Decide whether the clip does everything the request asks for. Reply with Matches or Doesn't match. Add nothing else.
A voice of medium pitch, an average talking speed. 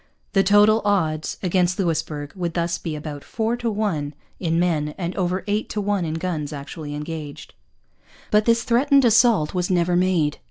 Matches